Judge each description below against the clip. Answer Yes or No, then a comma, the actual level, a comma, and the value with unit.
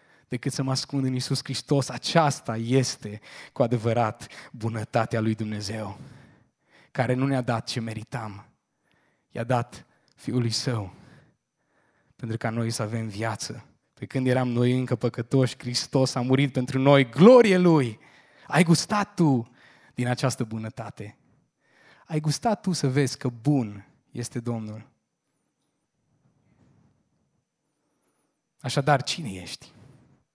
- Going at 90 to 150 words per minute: Yes, average, 120 wpm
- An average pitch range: Yes, average, 3.1 semitones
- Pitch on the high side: No, low, 125 Hz